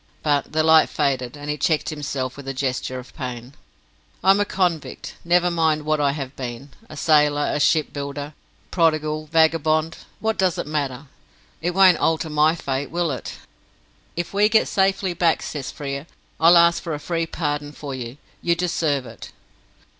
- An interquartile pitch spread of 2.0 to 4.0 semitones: Yes, average, 3.2 semitones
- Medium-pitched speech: Yes, medium, 155 Hz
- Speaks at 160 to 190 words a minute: Yes, average, 175 wpm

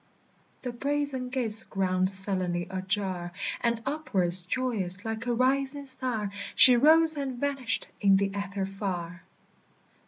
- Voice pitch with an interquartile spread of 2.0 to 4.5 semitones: No, average, 5.3 semitones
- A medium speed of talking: No, slow, 125 wpm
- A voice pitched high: Yes, high, 220 Hz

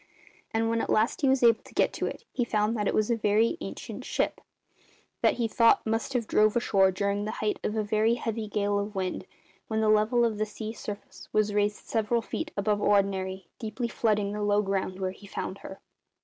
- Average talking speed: No, fast, 220 wpm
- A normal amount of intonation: No, narrow, 1.9 semitones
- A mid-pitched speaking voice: No, high, 215 Hz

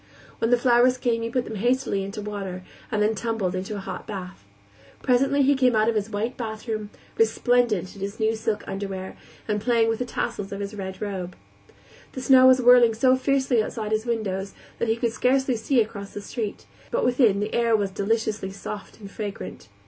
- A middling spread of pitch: Yes, average, 3.3 semitones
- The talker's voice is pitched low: No, high, 220 Hz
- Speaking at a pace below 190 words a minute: No, average, 200 wpm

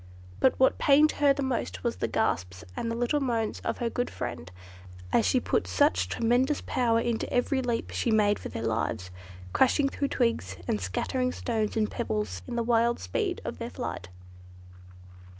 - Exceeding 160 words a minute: Yes, average, 170 wpm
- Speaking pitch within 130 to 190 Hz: No, high, 230 Hz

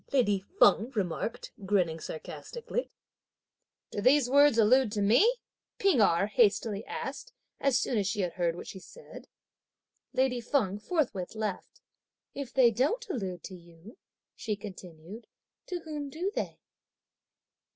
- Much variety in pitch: Yes, wide, 6.3 semitones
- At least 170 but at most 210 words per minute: No, slow, 135 wpm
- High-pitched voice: Yes, high, 220 Hz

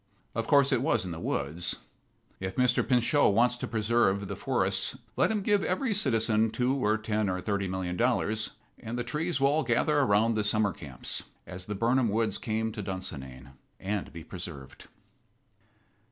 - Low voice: Yes, low, 110 Hz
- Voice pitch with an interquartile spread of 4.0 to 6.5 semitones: Yes, average, 4.7 semitones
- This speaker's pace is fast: No, average, 175 wpm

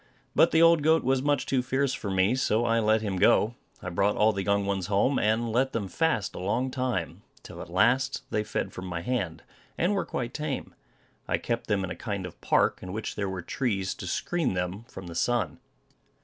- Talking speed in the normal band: No, fast, 220 wpm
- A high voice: No, low, 110 Hz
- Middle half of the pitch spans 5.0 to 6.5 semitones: Yes, average, 5.3 semitones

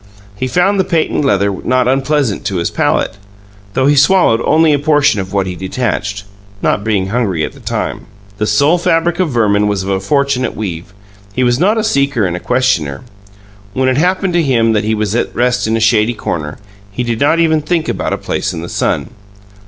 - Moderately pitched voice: No, low, 125 Hz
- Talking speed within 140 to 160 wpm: No, fast, 205 wpm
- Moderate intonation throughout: No, wide, 6.4 semitones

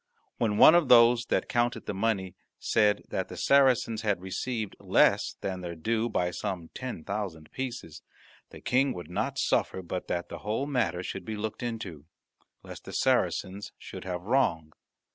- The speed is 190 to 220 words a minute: No, average, 170 wpm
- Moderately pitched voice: No, low, 105 Hz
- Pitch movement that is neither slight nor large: Yes, average, 4.9 semitones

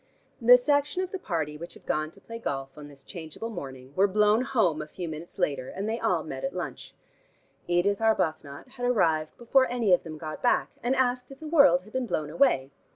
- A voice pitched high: Yes, high, 195 Hz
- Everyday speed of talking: No, fast, 220 wpm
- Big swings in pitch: Yes, wide, 8.1 semitones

